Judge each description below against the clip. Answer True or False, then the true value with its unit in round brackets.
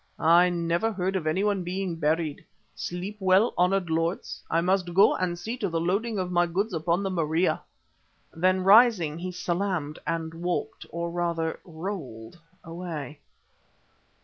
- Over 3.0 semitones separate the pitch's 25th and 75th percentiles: False (2.4 semitones)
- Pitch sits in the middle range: True (175 Hz)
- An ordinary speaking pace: True (150 wpm)